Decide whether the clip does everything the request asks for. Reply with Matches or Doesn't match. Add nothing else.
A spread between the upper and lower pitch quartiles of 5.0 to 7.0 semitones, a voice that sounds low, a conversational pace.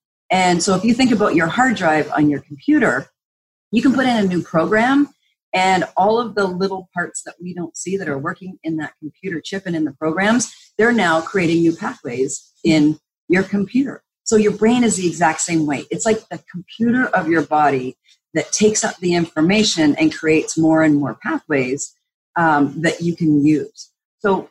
Doesn't match